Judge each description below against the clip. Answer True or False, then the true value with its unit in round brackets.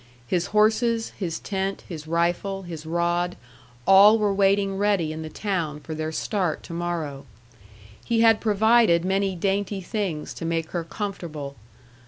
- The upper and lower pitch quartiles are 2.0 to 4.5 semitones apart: True (3.6 semitones)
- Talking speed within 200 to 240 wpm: False (150 wpm)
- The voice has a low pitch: False (185 Hz)